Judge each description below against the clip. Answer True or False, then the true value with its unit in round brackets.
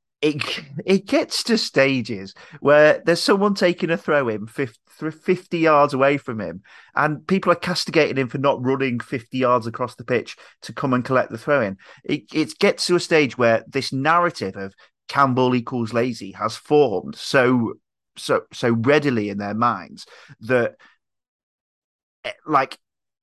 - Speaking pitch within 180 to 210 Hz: False (140 Hz)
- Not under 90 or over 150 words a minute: False (160 wpm)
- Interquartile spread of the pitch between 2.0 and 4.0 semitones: False (4.8 semitones)